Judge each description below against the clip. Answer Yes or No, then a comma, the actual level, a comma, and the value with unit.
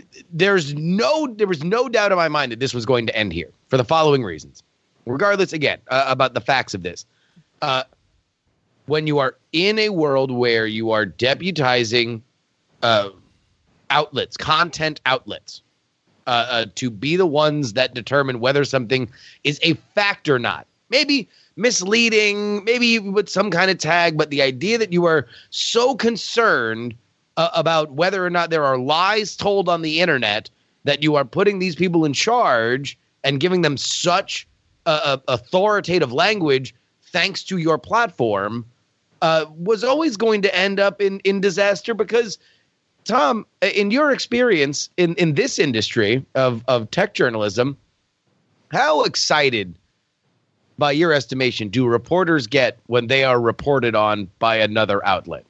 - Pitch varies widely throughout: Yes, wide, 7.3 semitones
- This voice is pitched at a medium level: Yes, medium, 150 Hz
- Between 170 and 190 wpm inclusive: No, average, 155 wpm